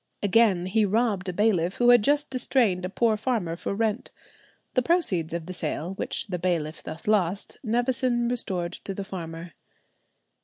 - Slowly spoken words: No, average, 165 wpm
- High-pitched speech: Yes, high, 200 Hz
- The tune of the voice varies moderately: Yes, average, 5.0 semitones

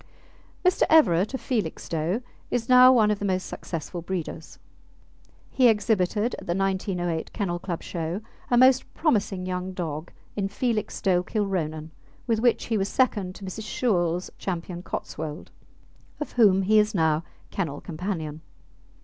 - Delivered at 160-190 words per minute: No, average, 140 wpm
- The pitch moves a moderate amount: Yes, average, 4.2 semitones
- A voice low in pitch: No, high, 190 Hz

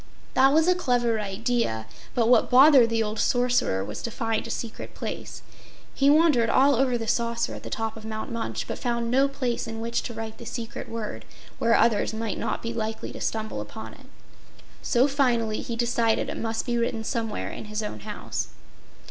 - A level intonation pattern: Yes, narrow, 1.9 semitones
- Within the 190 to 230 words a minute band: Yes, average, 200 wpm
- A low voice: No, high, 230 Hz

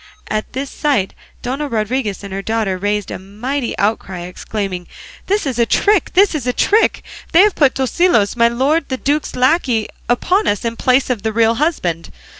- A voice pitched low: No, high, 240 Hz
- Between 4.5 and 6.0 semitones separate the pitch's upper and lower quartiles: Yes, wide, 5.6 semitones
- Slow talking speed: No, average, 185 wpm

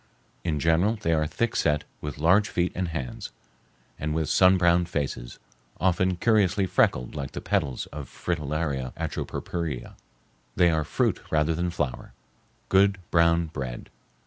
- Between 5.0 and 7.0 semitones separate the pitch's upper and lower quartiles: No, average, 3.3 semitones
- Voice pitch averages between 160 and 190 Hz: No, very low, 85 Hz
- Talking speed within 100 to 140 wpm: Yes, slow, 135 wpm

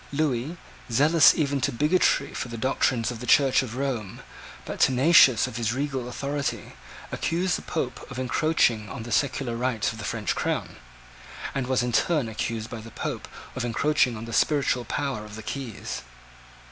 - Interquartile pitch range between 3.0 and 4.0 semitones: Yes, average, 3.4 semitones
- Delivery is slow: No, average, 175 wpm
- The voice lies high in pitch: No, low, 125 Hz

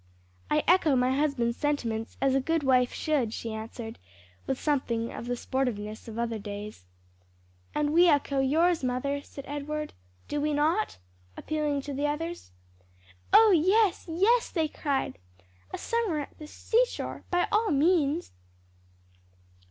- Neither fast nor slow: Yes, average, 145 wpm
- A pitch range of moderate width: Yes, average, 4.5 semitones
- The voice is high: Yes, very high, 290 Hz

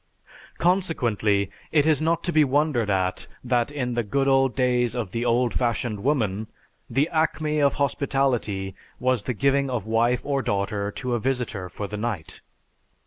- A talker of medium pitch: No, low, 125 Hz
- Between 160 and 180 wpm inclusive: Yes, average, 165 wpm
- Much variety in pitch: No, average, 4.5 semitones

